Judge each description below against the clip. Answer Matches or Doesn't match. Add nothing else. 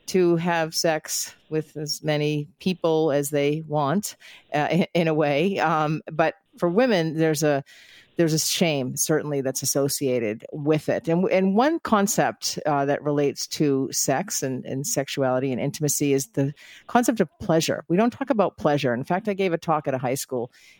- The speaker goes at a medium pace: Matches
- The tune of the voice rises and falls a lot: Doesn't match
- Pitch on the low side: Doesn't match